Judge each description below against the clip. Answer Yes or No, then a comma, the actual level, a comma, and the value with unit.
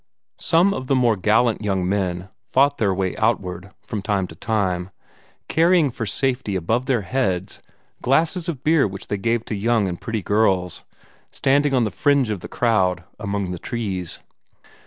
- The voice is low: Yes, low, 110 Hz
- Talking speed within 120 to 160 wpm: No, average, 170 wpm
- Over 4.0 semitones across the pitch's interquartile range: Yes, wide, 5.5 semitones